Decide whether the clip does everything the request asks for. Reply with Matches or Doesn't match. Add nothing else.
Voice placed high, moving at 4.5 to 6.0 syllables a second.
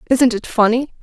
Matches